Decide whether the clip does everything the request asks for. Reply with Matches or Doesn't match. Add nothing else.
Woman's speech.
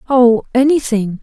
Matches